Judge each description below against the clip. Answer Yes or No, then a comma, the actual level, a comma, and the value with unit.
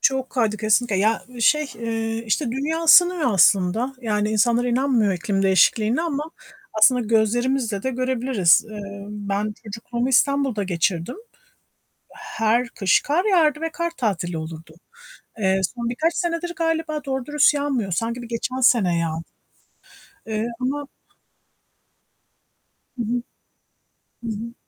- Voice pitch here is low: No, high, 235 Hz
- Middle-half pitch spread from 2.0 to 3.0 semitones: No, average, 4.5 semitones